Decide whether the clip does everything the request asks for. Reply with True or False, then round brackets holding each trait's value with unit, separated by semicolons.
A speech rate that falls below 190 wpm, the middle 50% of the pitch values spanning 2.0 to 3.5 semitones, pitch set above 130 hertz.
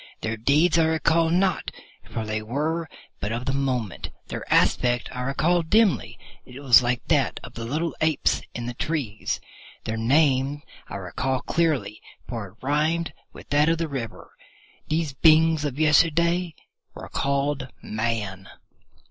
False (155 wpm; 5.2 semitones; 140 Hz)